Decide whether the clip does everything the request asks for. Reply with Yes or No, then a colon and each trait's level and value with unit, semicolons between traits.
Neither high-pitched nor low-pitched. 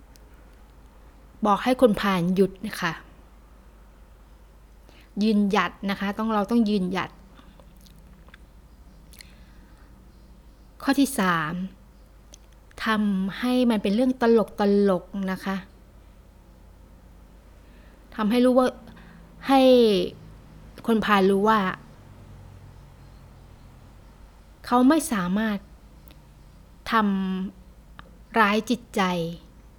Yes: medium, 180 Hz